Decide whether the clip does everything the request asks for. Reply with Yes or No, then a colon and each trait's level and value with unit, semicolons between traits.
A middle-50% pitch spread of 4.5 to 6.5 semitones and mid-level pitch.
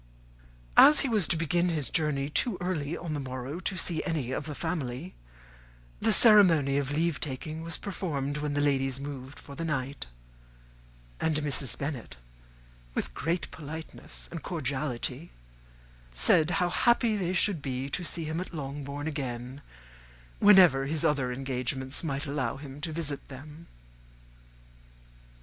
No: average, 3.6 semitones; medium, 150 Hz